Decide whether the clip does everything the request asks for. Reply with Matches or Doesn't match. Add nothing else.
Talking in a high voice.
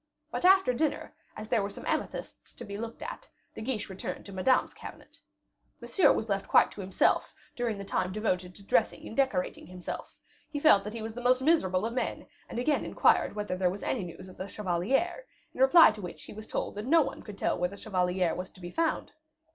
Matches